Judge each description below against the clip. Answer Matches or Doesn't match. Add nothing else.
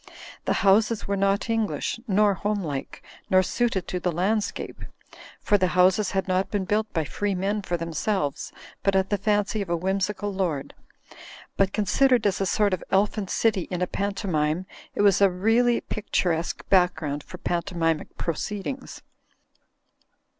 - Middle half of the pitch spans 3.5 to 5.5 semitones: Doesn't match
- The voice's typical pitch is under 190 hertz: Doesn't match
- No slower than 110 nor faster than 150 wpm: Doesn't match